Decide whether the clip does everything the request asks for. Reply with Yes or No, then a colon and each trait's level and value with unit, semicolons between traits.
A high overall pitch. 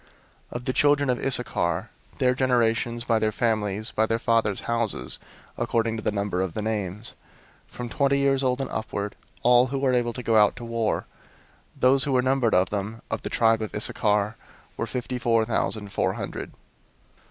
No: low, 115 Hz